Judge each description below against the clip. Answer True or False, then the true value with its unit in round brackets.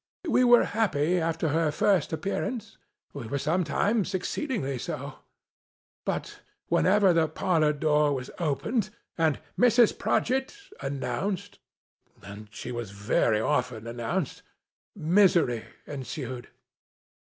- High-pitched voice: False (160 Hz)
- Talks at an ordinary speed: False (115 wpm)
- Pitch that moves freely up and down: True (6.6 semitones)